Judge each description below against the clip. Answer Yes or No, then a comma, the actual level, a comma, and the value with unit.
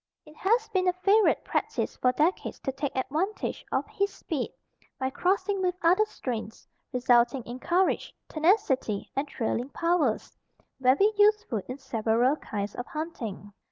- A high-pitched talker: Yes, very high, 290 Hz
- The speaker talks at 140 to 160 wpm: Yes, average, 150 wpm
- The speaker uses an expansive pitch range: Yes, wide, 7.1 semitones